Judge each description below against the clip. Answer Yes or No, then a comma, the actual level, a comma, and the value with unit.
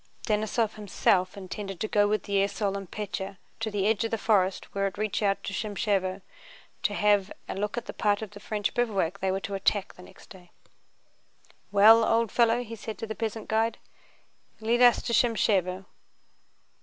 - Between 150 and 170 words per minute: No, average, 180 wpm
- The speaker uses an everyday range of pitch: No, narrow, 2.2 semitones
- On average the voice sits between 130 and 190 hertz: No, high, 205 Hz